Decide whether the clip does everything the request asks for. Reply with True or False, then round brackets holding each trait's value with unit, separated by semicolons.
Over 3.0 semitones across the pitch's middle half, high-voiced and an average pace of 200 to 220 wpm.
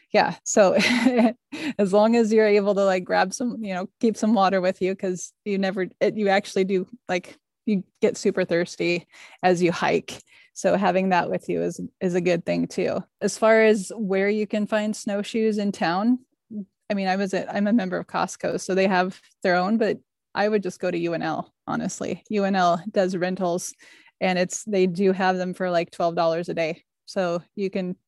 False (2.7 semitones; 195 Hz; 205 wpm)